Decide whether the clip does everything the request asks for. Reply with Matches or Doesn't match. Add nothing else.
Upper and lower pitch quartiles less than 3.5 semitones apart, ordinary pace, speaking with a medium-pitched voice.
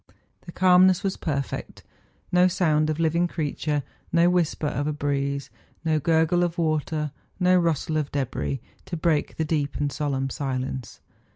Matches